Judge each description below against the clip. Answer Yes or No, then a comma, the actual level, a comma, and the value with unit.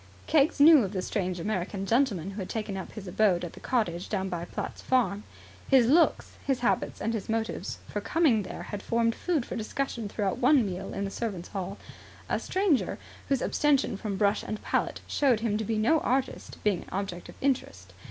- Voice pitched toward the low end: No, high, 215 Hz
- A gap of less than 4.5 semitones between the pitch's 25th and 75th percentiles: No, average, 4.8 semitones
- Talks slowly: No, average, 200 wpm